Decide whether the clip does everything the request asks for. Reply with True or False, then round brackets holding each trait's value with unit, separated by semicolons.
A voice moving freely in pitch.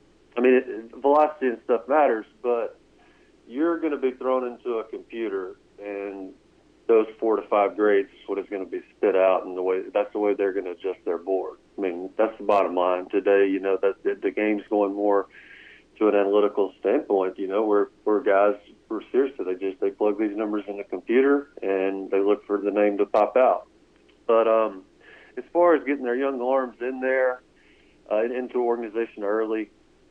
True (9.0 semitones)